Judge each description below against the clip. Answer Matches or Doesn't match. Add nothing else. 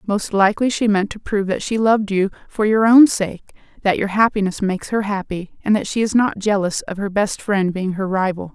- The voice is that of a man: Doesn't match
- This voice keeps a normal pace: Doesn't match